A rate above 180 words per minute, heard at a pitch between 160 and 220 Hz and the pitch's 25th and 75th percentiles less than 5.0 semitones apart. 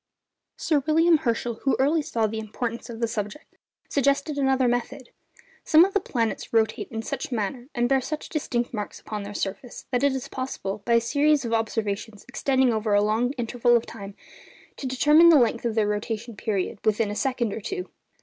No: average, 200 wpm; high, 240 Hz; average, 3.7 semitones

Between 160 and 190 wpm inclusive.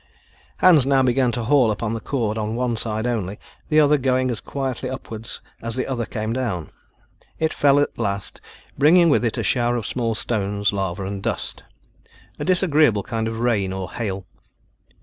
Yes: average, 180 wpm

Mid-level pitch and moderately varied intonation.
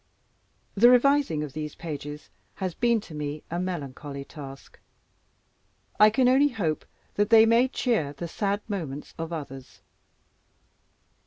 No: medium, 170 Hz; wide, 7.3 semitones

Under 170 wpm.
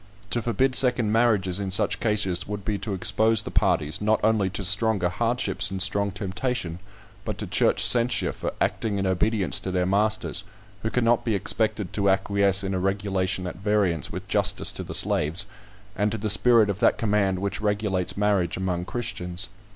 No: average, 180 wpm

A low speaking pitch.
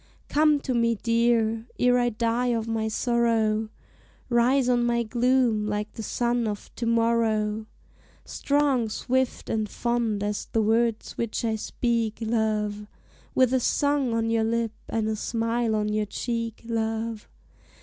No: high, 230 Hz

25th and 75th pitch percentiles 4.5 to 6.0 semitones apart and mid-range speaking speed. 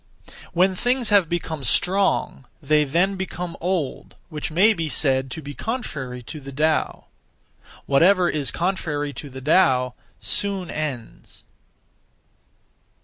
No: average, 5.2 semitones; slow, 125 wpm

